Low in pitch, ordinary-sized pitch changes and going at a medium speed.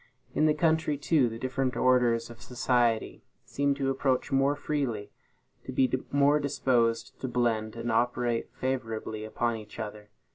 Yes: low, 125 Hz; average, 3.1 semitones; average, 150 wpm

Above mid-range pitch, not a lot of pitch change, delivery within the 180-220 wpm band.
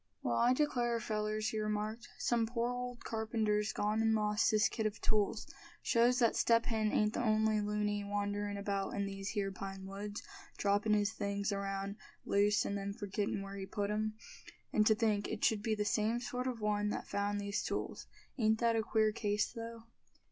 Yes: high, 210 Hz; narrow, 1.6 semitones; average, 190 wpm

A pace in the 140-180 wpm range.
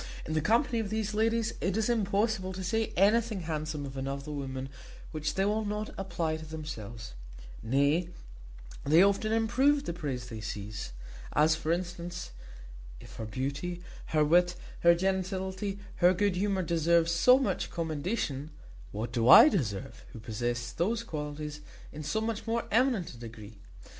Yes: average, 160 wpm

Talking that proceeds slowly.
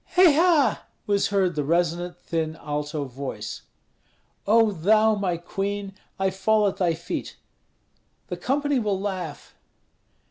Yes: slow, 130 wpm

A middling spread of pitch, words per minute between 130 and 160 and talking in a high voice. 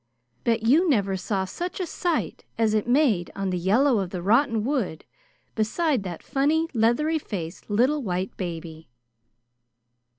No: wide, 7.1 semitones; average, 145 wpm; high, 220 Hz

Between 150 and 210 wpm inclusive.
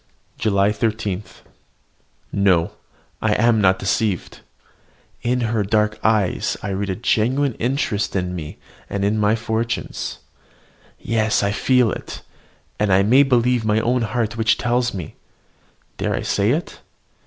No: average, 140 wpm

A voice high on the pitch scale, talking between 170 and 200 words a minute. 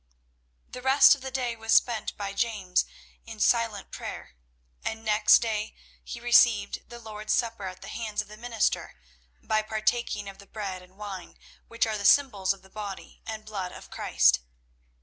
Yes: high, 215 Hz; average, 175 wpm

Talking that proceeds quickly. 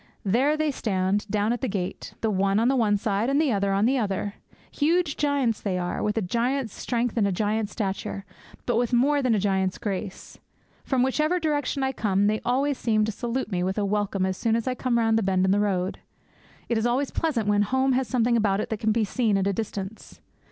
Yes: fast, 235 wpm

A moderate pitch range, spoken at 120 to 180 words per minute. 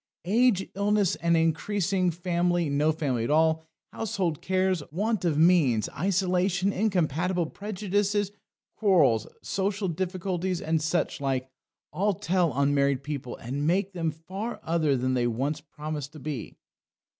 Yes: average, 4.2 semitones; slow, 135 wpm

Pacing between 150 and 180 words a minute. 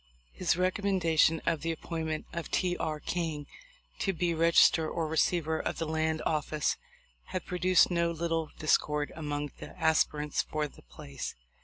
Yes: average, 165 wpm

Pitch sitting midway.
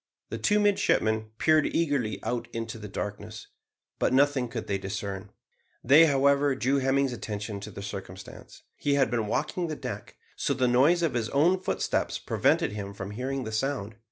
No: low, 125 Hz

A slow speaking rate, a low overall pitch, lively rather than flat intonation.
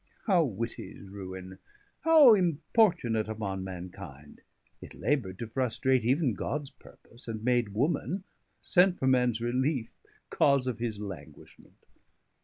Yes: slow, 125 wpm; low, 120 Hz; wide, 5.9 semitones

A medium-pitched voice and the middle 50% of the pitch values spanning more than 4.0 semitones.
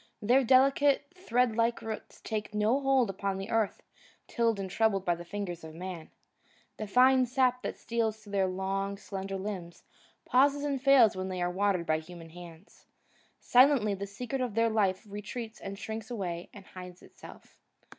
No: high, 210 Hz; average, 4.5 semitones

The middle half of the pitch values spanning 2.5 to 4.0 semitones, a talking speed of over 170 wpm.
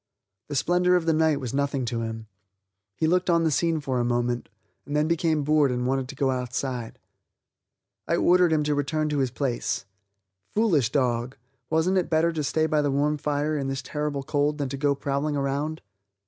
Yes: average, 2.9 semitones; average, 200 wpm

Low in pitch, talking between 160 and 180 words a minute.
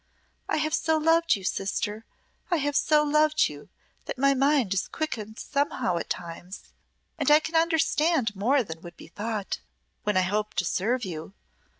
No: very high, 250 Hz; average, 175 wpm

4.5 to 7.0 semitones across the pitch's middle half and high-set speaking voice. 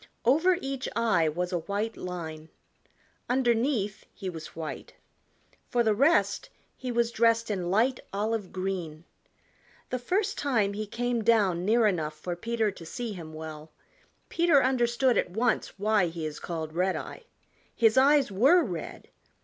Yes: wide, 5.5 semitones; high, 215 Hz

